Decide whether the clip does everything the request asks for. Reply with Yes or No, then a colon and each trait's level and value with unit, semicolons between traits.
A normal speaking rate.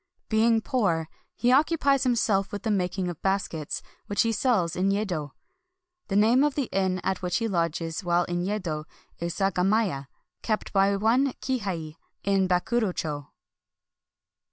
Yes: average, 155 wpm